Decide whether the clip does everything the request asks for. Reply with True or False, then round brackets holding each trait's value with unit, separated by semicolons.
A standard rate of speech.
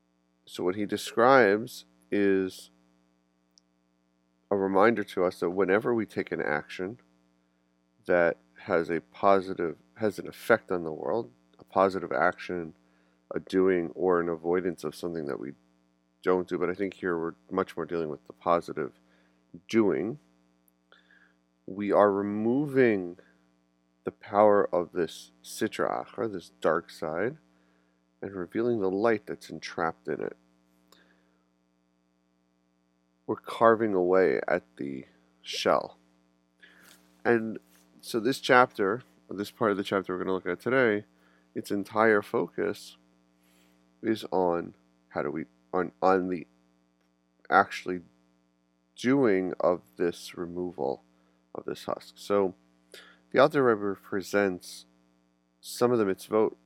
False (125 wpm)